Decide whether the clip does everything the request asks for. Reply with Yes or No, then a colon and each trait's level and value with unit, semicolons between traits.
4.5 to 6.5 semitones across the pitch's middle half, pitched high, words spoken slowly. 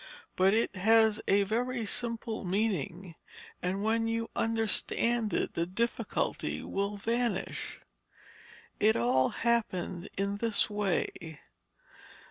No: average, 3.3 semitones; high, 210 Hz; slow, 105 wpm